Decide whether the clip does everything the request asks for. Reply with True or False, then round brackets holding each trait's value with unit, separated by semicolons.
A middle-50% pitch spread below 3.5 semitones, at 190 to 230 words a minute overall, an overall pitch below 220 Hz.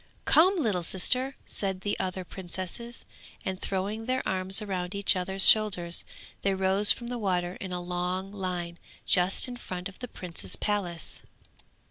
False (2.7 semitones; 155 wpm; 190 Hz)